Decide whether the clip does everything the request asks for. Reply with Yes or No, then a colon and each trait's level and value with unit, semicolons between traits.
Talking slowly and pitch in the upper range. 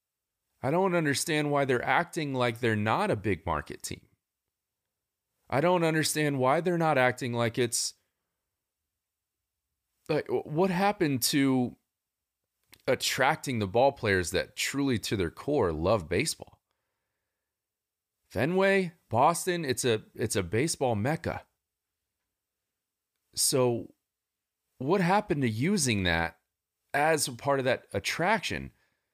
No: slow, 115 wpm; low, 125 Hz